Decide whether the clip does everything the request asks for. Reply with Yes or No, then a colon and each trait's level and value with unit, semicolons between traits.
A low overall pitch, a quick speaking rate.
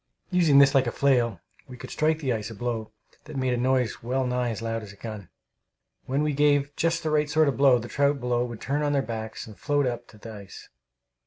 Yes: low, 125 Hz; fast, 245 wpm